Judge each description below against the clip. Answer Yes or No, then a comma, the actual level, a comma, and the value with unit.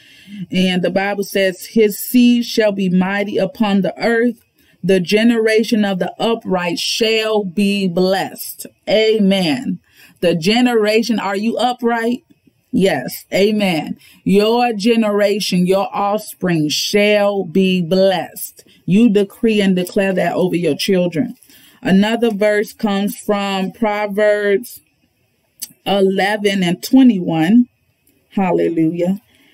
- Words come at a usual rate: No, slow, 105 wpm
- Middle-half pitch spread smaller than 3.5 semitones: Yes, narrow, 2.6 semitones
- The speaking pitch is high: Yes, high, 205 Hz